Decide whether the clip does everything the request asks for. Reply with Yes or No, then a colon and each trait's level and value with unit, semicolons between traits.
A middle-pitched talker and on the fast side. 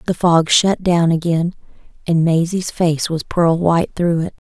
No: medium, 170 Hz; average, 175 wpm